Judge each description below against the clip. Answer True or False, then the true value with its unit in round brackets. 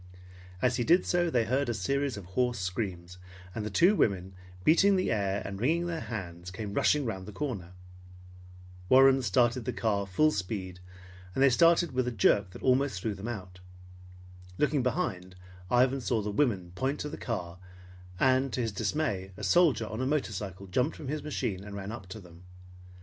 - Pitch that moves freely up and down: True (6.0 semitones)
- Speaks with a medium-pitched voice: False (115 Hz)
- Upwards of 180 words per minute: True (190 wpm)